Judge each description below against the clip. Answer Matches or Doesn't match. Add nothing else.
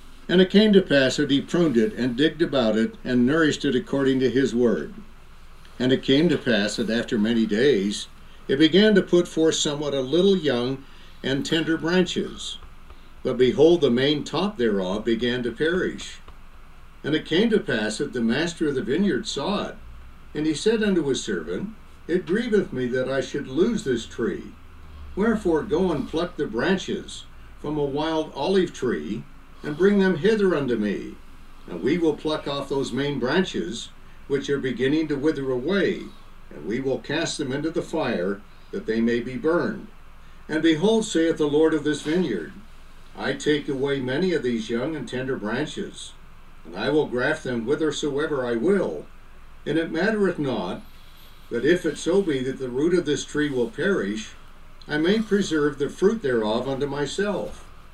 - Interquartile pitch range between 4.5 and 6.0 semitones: Matches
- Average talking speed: Matches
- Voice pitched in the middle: Matches